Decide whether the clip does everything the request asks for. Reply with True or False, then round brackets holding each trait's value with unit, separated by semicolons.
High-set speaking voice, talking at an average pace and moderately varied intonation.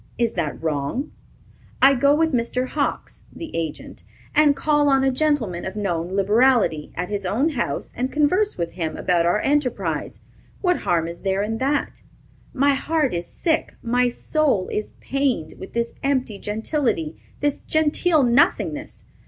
False (245 Hz; 155 wpm; 7.3 semitones)